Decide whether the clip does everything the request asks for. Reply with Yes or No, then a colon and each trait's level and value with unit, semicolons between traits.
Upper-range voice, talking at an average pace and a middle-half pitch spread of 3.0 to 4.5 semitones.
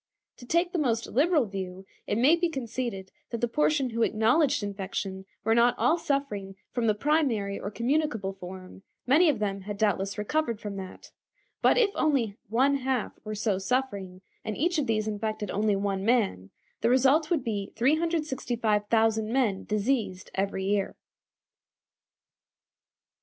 No: high, 225 Hz; average, 150 wpm; average, 5.2 semitones